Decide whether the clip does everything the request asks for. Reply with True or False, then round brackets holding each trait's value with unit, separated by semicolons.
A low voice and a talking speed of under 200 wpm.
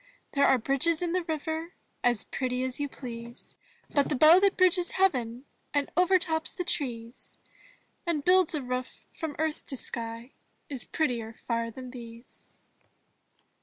False (280 Hz; 150 wpm)